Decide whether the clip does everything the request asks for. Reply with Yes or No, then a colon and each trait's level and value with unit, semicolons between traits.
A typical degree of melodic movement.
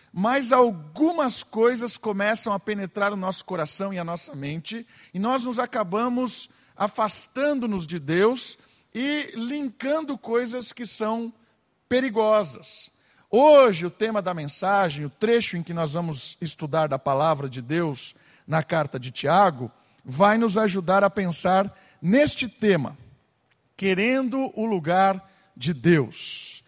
No: wide, 5.9 semitones